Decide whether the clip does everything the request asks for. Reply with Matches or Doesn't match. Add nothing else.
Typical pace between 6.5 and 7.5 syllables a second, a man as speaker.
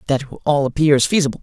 Matches